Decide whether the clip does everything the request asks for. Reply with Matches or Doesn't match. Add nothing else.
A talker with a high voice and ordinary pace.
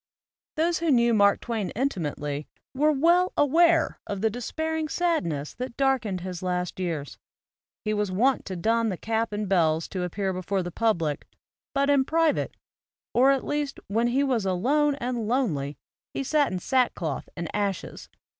Matches